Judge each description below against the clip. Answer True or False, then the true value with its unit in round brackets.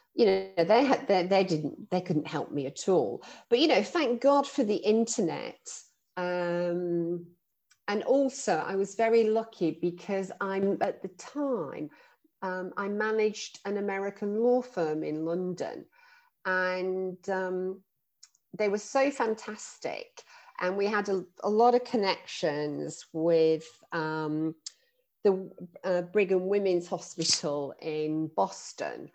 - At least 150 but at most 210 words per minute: False (135 wpm)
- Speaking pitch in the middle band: False (195 Hz)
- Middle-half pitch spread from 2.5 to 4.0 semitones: False (4.4 semitones)